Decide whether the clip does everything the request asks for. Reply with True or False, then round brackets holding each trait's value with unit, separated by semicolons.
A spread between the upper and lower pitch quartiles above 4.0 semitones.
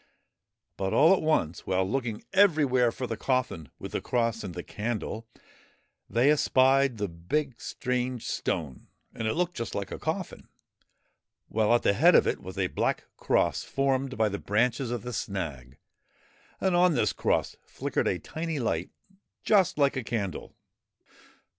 True (5.0 semitones)